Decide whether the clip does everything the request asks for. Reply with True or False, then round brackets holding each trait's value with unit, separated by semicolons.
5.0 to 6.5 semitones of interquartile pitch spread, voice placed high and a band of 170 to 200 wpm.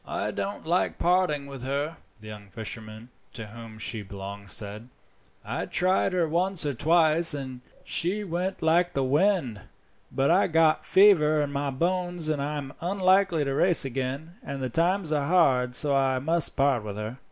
False (5.4 semitones; 145 Hz; 175 wpm)